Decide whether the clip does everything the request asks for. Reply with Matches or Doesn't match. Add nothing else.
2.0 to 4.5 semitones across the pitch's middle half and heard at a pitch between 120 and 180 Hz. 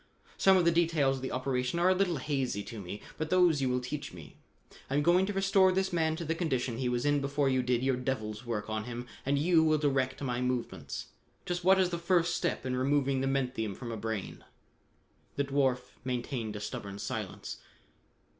Doesn't match